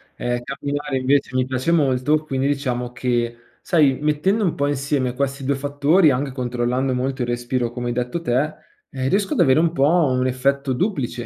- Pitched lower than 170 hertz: Yes, low, 135 Hz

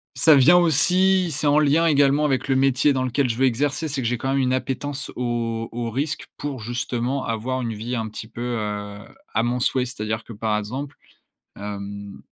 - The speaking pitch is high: No, low, 130 Hz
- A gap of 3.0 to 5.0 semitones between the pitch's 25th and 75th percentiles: Yes, average, 3.8 semitones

